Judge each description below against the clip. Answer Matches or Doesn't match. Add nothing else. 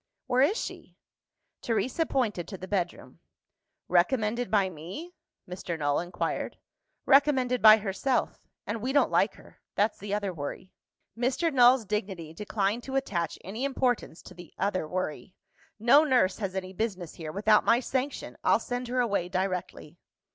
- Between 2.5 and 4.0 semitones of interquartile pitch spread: Doesn't match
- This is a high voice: Matches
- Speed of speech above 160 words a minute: Doesn't match